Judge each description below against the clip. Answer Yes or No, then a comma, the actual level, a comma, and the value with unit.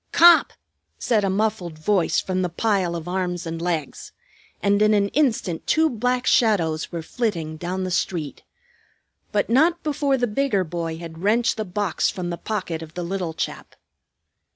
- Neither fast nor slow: Yes, average, 170 wpm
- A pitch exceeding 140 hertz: Yes, high, 190 Hz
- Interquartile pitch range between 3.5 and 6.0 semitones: Yes, average, 4.5 semitones